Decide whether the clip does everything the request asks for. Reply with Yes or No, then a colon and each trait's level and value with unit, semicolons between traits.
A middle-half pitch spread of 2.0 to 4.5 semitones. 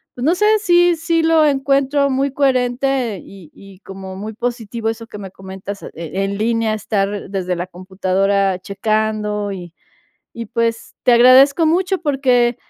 No: wide, 5.6 semitones